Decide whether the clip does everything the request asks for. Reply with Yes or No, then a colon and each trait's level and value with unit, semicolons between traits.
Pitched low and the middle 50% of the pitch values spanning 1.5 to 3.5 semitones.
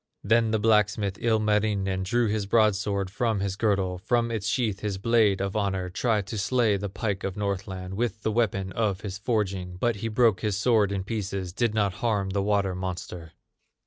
Yes: low, 100 Hz; narrow, 2.4 semitones